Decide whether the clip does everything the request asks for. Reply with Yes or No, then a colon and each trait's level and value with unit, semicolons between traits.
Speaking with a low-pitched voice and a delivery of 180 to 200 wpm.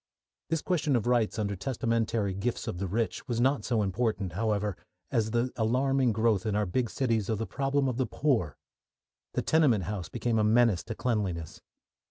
Yes: low, 115 Hz; average, 185 wpm